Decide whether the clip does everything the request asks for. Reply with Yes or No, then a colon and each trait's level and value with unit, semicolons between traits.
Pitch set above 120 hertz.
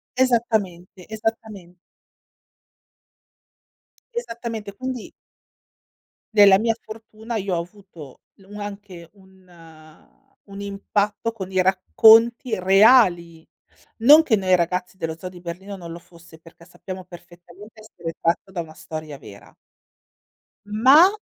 Yes: high, 190 Hz